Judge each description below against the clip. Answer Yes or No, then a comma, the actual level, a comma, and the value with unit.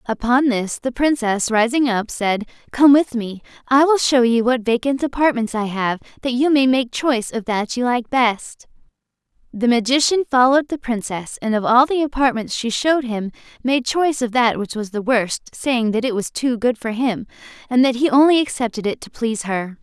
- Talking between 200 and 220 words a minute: Yes, fast, 205 wpm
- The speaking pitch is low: No, high, 245 Hz